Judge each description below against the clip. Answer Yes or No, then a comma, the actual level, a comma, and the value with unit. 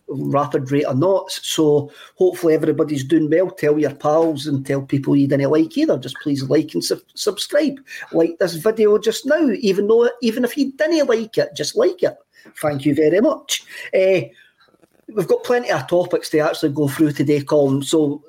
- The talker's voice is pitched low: No, medium, 160 Hz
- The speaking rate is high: No, average, 190 wpm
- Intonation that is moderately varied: No, wide, 7.4 semitones